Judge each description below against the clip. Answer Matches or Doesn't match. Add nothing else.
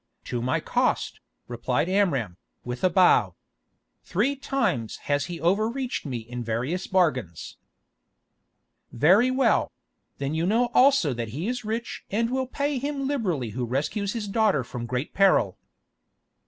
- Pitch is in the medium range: Matches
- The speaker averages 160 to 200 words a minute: Doesn't match